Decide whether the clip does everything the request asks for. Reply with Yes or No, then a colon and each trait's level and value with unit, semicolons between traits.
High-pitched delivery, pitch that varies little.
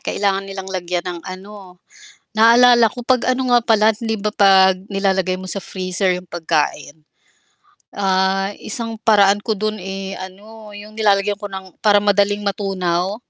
Yes: high, 195 Hz; narrow, 2.3 semitones